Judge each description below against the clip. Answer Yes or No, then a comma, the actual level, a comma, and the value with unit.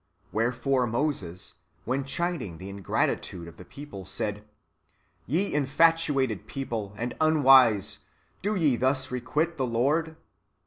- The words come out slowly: Yes, slow, 125 wpm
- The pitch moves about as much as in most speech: No, wide, 5.9 semitones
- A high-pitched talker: No, low, 130 Hz